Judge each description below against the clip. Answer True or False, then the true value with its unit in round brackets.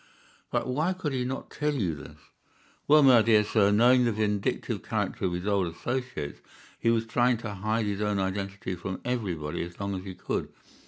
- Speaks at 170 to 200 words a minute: True (195 wpm)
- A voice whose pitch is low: True (105 Hz)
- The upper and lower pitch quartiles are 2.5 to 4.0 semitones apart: False (4.5 semitones)